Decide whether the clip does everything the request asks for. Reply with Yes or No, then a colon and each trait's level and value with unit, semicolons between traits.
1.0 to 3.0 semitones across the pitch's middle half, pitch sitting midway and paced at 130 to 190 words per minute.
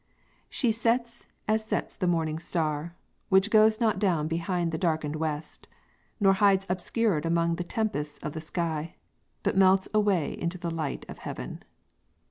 No: average, 4.4 semitones; medium, 175 Hz; average, 155 wpm